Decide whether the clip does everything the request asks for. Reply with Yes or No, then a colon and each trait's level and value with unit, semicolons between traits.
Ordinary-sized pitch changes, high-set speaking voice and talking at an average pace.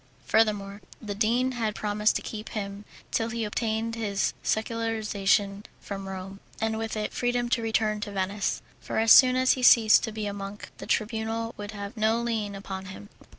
No: narrow, 2.0 semitones; high, 215 Hz; average, 185 wpm